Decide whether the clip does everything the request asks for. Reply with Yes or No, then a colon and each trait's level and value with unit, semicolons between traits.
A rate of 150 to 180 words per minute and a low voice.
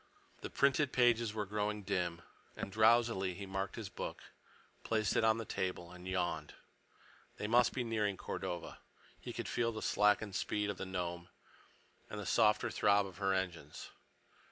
Yes: average, 165 wpm; low, 105 Hz